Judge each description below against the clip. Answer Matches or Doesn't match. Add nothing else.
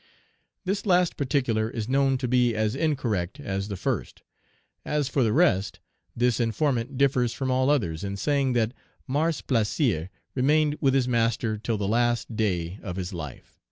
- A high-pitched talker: Doesn't match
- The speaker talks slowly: Doesn't match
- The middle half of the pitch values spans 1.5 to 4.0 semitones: Doesn't match